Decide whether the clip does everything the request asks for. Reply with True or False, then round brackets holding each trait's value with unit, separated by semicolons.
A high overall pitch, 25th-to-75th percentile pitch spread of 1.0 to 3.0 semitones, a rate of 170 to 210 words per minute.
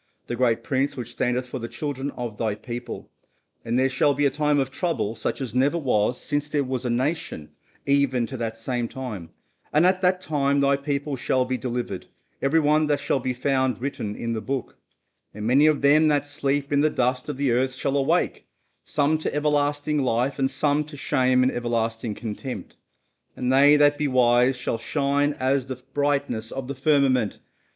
False (135 Hz; 2.6 semitones; 195 wpm)